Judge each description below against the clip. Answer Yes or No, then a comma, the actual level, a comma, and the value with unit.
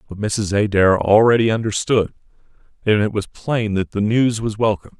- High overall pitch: No, low, 105 Hz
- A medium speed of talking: Yes, average, 170 wpm